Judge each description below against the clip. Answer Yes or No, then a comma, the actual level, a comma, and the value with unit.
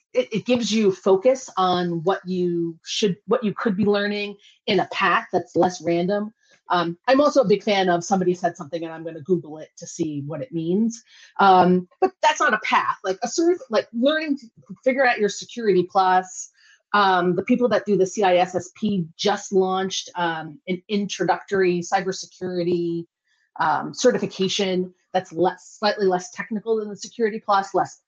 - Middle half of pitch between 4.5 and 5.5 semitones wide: No, average, 2.9 semitones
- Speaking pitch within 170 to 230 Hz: Yes, high, 190 Hz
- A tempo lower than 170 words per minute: No, average, 175 wpm